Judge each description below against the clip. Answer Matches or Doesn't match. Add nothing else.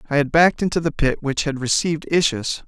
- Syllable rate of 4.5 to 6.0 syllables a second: Doesn't match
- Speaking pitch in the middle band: Matches